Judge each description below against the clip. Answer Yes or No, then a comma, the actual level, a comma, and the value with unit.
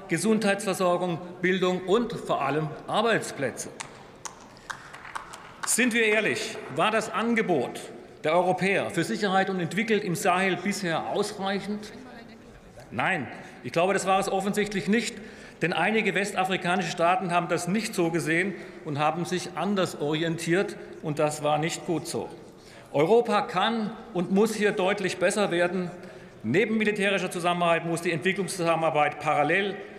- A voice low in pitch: No, medium, 185 Hz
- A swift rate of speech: No, average, 130 wpm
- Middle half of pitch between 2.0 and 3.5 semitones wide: Yes, average, 3.0 semitones